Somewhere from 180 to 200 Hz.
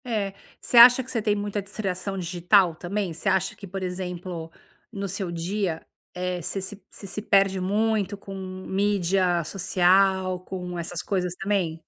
Yes: high, 190 Hz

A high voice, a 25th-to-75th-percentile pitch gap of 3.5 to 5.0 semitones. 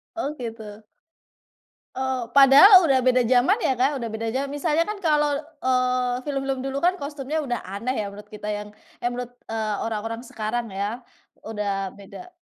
Yes: very high, 250 Hz; average, 3.8 semitones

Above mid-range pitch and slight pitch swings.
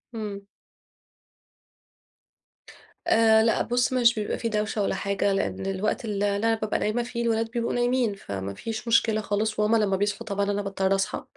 Yes: high, 215 Hz; narrow, 2.3 semitones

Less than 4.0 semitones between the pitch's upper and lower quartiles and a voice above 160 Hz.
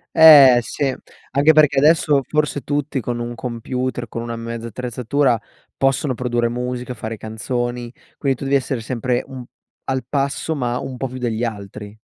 No: narrow, 2.5 semitones; low, 125 Hz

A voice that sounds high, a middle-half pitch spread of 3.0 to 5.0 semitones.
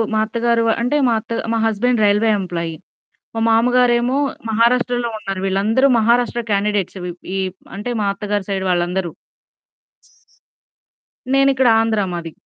Yes: high, 225 Hz; average, 3.6 semitones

